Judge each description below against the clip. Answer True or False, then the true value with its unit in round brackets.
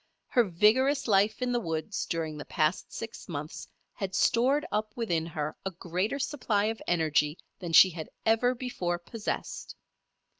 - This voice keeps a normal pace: True (155 wpm)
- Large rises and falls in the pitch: True (5.8 semitones)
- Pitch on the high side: True (195 Hz)